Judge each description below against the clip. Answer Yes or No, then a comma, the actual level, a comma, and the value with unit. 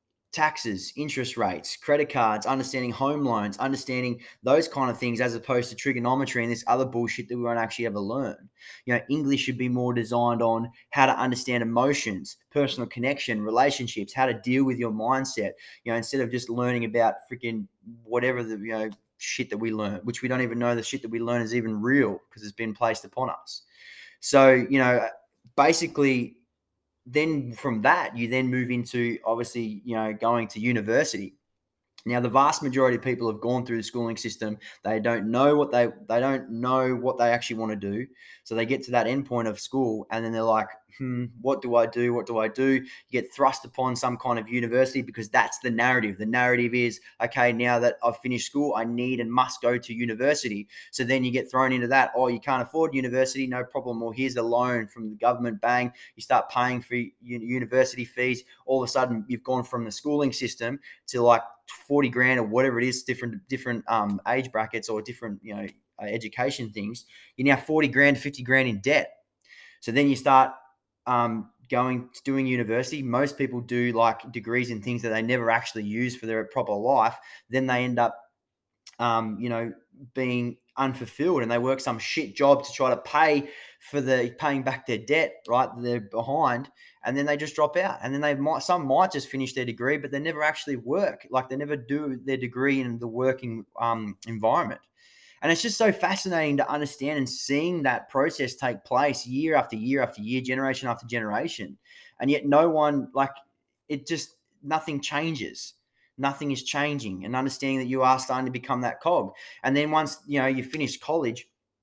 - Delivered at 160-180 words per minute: No, fast, 205 wpm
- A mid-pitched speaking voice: No, low, 125 Hz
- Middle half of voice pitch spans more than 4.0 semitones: No, narrow, 2.5 semitones